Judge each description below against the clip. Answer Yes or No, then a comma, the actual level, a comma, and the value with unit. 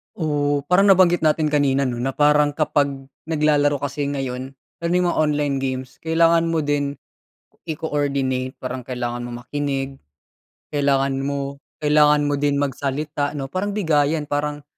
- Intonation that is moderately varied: No, narrow, 1.9 semitones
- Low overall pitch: No, medium, 145 Hz